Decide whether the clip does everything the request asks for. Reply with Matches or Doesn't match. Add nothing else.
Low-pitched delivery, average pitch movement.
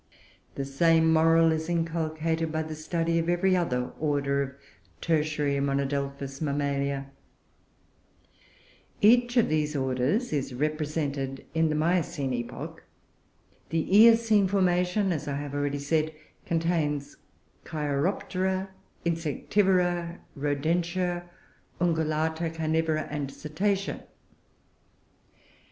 Doesn't match